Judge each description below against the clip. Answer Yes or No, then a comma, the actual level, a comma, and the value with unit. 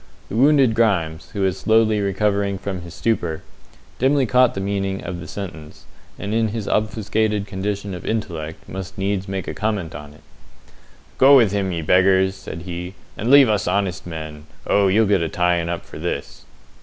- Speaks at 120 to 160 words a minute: No, average, 180 wpm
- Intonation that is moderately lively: Yes, average, 3.5 semitones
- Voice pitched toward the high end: No, very low, 95 Hz